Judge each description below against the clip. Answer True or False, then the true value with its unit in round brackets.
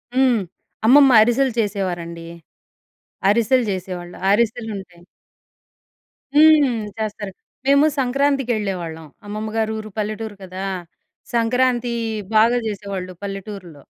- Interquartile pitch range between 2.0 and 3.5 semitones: False (4.1 semitones)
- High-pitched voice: True (215 Hz)